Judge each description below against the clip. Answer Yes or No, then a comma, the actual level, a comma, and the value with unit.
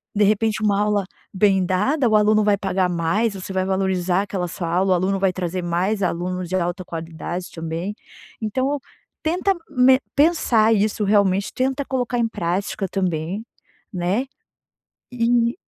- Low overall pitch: No, high, 195 Hz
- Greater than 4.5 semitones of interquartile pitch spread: No, average, 3.4 semitones